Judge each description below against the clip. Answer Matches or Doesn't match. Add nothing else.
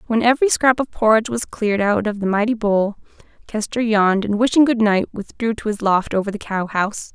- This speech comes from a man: Doesn't match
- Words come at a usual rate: Doesn't match